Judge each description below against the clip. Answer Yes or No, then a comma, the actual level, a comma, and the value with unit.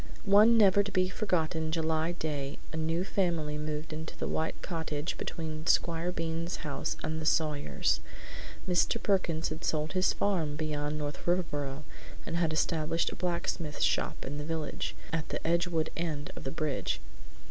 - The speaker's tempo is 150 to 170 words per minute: Yes, average, 160 wpm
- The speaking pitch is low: No, medium, 160 Hz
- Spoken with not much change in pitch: Yes, narrow, 2.2 semitones